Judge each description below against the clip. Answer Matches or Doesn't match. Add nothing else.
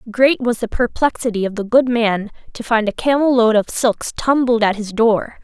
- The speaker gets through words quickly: Matches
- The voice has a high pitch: Matches